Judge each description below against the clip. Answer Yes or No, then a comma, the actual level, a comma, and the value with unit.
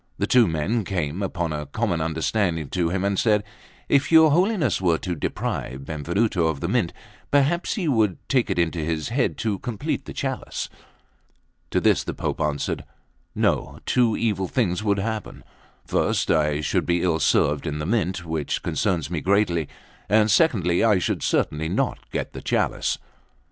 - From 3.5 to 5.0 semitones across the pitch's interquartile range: No, wide, 5.5 semitones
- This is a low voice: Yes, very low, 90 Hz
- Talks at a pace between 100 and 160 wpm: No, average, 170 wpm